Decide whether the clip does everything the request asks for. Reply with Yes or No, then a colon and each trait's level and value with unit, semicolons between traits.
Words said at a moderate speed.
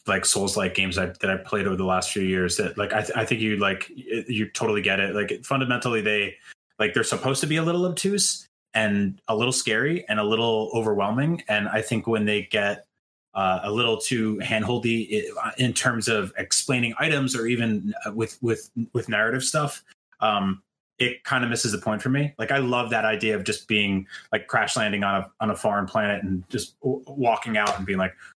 No: fast, 220 wpm